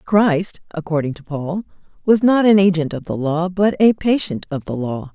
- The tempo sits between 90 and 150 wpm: No, average, 200 wpm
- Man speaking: No, female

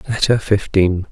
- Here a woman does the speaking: No, male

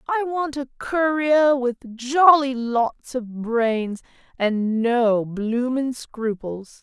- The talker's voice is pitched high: Yes, very high, 250 Hz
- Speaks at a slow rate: Yes, slow, 115 wpm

